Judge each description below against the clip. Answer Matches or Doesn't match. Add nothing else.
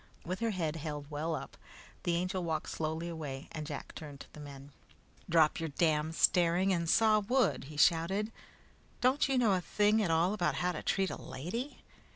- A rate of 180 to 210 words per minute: Matches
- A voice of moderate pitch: Matches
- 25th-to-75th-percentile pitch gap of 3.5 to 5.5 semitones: Matches